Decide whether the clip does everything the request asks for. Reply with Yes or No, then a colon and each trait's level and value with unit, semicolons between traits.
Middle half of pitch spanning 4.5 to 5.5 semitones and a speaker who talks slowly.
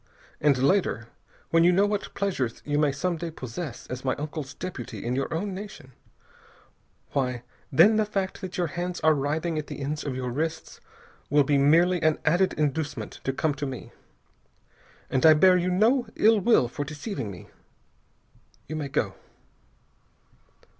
No: average, 5.0 semitones; average, 165 wpm